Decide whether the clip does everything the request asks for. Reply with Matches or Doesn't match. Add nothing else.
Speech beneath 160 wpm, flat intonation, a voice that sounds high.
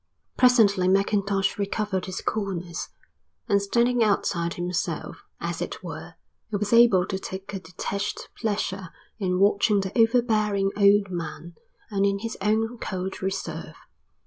Matches